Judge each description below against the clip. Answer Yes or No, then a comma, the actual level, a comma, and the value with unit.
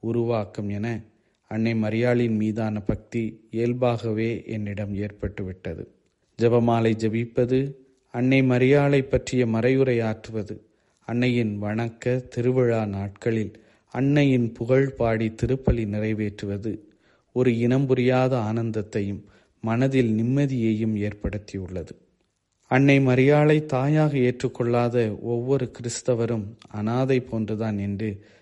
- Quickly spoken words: No, average, 80 wpm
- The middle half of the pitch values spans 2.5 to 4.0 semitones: Yes, average, 2.8 semitones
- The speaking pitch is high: No, low, 115 Hz